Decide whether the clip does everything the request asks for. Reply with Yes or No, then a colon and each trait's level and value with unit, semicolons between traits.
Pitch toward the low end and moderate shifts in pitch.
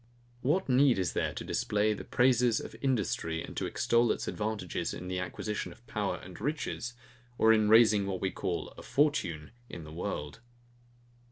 Yes: low, 105 Hz; average, 4.9 semitones